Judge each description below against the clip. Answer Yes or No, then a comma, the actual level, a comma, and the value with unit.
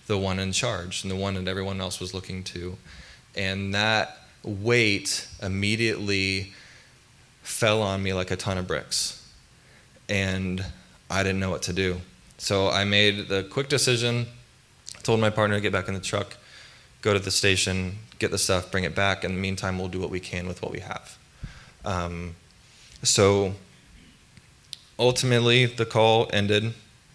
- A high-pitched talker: No, low, 100 Hz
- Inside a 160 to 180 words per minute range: Yes, average, 170 wpm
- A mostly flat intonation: No, average, 3.1 semitones